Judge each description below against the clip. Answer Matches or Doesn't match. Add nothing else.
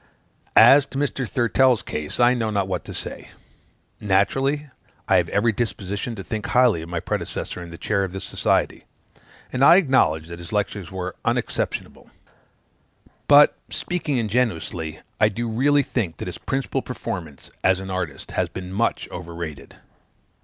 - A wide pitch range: Matches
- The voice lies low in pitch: Matches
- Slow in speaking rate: Doesn't match